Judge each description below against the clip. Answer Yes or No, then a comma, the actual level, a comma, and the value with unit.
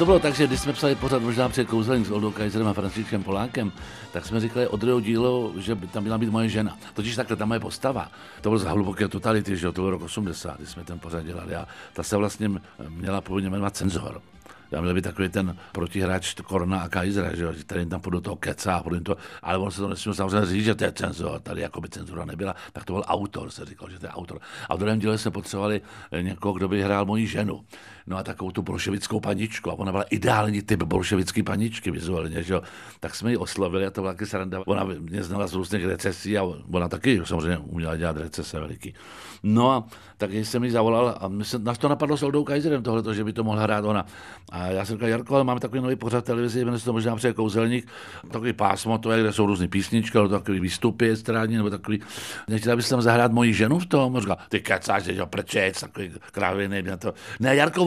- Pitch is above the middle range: No, low, 105 Hz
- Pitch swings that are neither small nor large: Yes, average, 3.2 semitones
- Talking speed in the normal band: No, fast, 225 wpm